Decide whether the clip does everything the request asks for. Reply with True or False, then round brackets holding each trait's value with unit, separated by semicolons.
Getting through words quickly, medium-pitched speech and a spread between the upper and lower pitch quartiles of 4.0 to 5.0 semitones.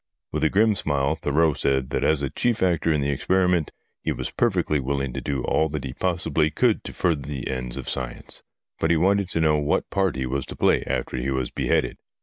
False (225 wpm; 75 Hz; 4.5 semitones)